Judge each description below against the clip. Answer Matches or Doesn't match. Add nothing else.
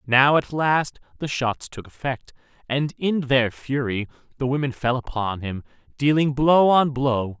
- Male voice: Matches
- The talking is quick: Doesn't match